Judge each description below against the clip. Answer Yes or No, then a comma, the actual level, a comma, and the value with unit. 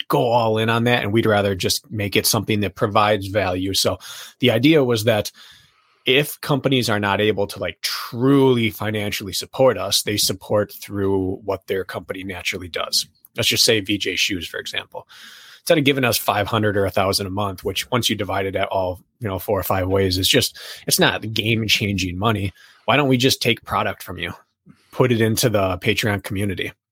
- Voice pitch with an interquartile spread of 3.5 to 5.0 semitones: No, average, 2.9 semitones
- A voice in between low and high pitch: No, low, 105 Hz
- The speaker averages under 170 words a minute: No, average, 200 wpm